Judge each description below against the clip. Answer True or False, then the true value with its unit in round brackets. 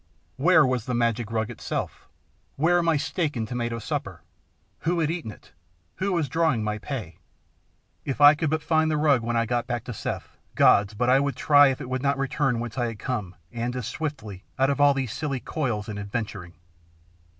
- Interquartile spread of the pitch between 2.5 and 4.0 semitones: False (4.5 semitones)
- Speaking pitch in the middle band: False (130 Hz)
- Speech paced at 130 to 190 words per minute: False (205 wpm)